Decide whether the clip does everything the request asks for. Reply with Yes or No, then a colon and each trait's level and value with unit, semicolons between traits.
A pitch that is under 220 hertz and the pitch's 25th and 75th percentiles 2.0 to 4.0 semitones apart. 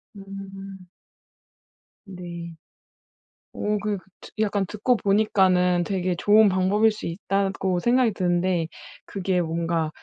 Yes: high, 190 Hz; narrow, 2.4 semitones